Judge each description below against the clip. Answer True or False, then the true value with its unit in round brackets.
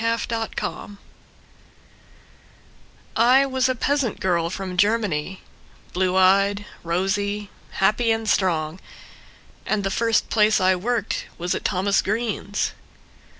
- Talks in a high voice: True (205 Hz)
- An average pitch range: True (3.3 semitones)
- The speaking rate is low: True (110 wpm)